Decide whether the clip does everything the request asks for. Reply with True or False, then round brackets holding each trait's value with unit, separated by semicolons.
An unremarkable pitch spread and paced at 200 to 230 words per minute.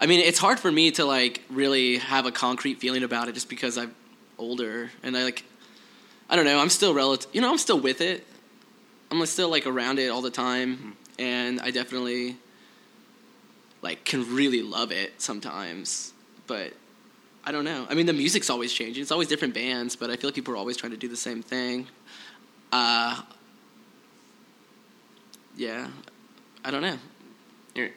False (3.6 semitones; 180 wpm)